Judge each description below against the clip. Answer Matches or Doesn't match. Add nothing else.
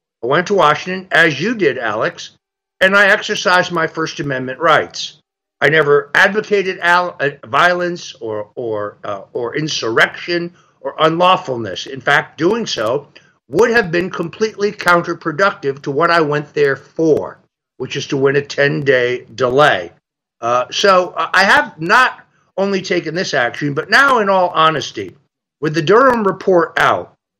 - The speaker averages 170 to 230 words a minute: Doesn't match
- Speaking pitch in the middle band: Matches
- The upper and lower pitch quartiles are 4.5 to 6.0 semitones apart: Matches